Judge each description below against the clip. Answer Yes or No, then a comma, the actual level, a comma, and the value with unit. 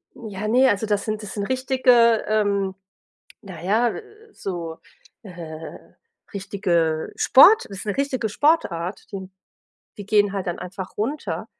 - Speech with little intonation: No, average, 3.6 semitones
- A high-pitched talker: Yes, high, 205 Hz